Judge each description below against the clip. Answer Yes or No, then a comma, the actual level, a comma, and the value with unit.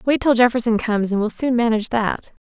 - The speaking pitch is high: Yes, high, 230 Hz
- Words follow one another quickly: Yes, fast, 220 wpm